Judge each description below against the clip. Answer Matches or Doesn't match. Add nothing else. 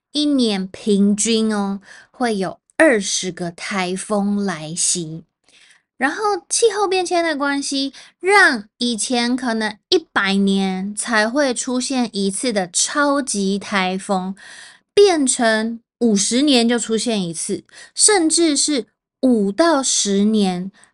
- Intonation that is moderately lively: Doesn't match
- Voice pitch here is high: Matches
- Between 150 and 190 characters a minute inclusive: Matches